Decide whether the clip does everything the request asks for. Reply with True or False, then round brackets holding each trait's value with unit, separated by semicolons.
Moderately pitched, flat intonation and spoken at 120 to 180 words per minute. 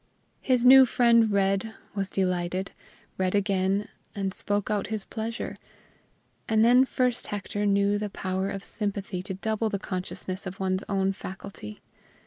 False (200 Hz; 2.3 semitones; 145 wpm)